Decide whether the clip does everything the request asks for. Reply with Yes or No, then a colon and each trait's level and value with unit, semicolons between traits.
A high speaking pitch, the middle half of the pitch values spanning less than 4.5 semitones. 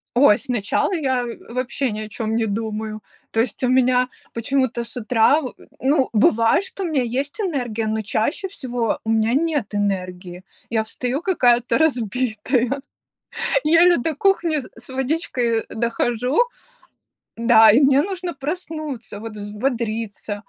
Yes: high, 245 Hz; average, 4.1 semitones